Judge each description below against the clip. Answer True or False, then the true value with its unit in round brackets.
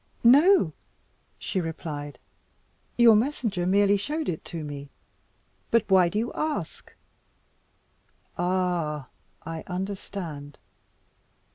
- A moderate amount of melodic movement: False (5.7 semitones)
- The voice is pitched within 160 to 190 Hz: True (185 Hz)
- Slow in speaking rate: True (95 wpm)